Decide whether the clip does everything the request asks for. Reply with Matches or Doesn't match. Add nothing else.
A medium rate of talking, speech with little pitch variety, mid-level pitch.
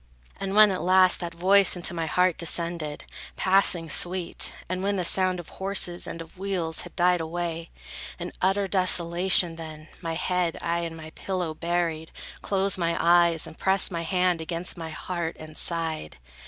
Matches